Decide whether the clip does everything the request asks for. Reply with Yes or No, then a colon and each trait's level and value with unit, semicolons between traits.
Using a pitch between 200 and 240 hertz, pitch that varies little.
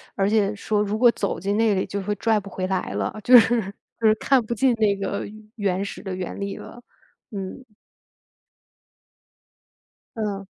Yes: high, 205 Hz; narrow, 2.1 semitones